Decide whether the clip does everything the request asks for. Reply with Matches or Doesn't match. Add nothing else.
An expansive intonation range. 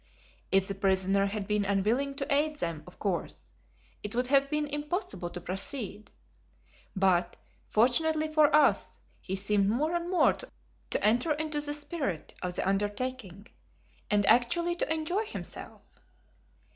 Matches